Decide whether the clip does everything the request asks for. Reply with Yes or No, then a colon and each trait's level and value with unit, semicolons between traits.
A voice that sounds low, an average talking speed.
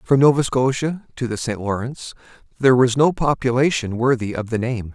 Yes: low, 125 Hz; average, 180 wpm